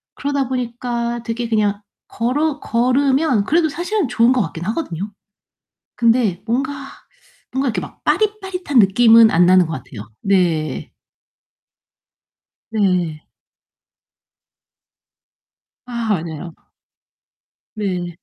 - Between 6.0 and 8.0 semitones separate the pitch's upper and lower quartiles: Yes, wide, 6.3 semitones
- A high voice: Yes, high, 230 Hz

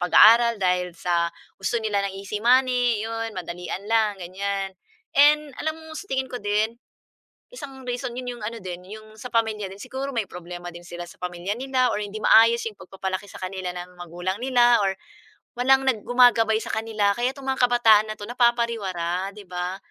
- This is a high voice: Yes, high, 215 Hz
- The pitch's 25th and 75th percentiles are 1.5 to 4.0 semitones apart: No, average, 4.5 semitones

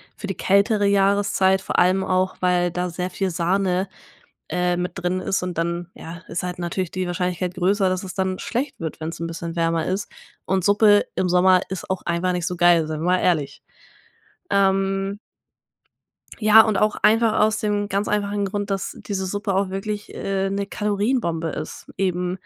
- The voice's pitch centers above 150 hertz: Yes, medium, 185 Hz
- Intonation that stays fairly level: Yes, narrow, 2.1 semitones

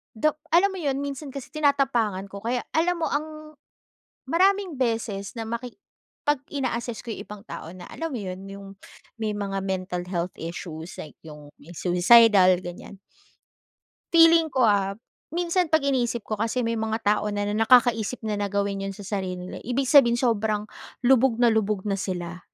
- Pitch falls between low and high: No, high, 225 Hz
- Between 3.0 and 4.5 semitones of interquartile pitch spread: No, wide, 5.6 semitones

